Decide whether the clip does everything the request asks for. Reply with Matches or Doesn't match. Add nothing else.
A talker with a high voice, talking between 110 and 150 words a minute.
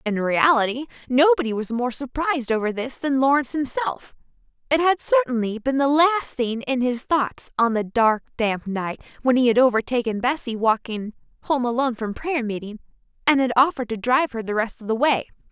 Doesn't match